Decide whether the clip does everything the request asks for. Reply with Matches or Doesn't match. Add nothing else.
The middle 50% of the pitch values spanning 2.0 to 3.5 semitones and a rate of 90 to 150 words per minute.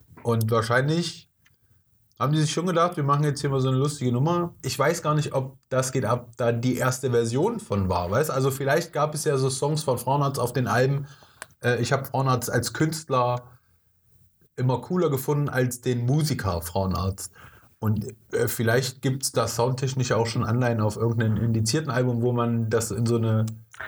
Doesn't match